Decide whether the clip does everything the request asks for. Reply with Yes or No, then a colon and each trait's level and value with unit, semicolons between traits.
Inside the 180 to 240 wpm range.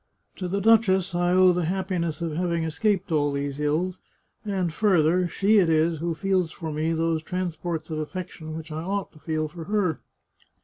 Yes: average, 190 wpm